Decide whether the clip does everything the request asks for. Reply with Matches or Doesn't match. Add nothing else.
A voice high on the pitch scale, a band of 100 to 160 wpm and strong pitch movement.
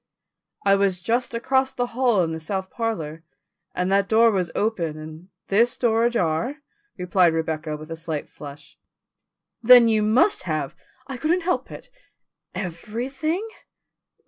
Matches